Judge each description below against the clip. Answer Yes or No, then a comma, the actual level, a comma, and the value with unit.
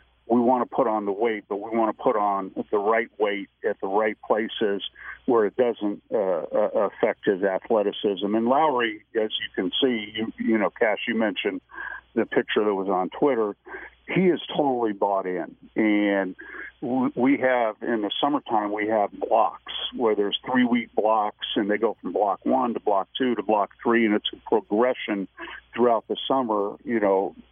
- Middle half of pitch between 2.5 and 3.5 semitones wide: Yes, average, 2.9 semitones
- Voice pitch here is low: Yes, low, 110 Hz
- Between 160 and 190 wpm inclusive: Yes, average, 185 wpm